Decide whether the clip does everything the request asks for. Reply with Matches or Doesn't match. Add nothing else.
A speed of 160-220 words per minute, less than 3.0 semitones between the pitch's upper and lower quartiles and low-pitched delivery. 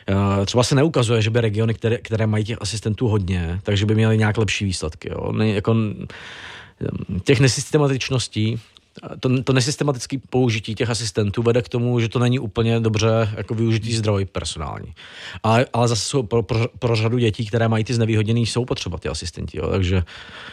Matches